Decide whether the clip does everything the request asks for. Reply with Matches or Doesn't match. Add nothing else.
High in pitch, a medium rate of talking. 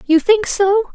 Matches